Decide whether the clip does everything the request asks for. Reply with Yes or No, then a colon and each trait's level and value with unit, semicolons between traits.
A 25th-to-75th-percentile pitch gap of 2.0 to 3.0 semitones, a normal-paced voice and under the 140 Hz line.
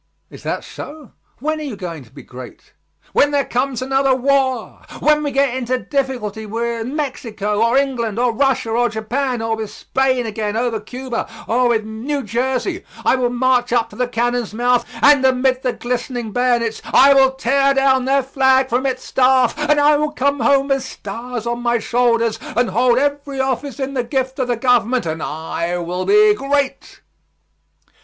No: average, 2.7 semitones; average, 180 wpm; very high, 250 Hz